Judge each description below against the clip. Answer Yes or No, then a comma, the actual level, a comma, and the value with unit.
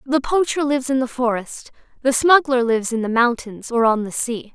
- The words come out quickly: Yes, fast, 210 wpm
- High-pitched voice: Yes, very high, 250 Hz